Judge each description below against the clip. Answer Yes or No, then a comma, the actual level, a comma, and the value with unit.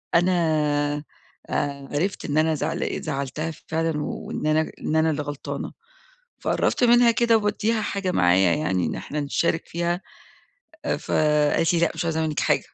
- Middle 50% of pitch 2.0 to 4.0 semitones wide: Yes, average, 3.1 semitones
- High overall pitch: No, medium, 160 Hz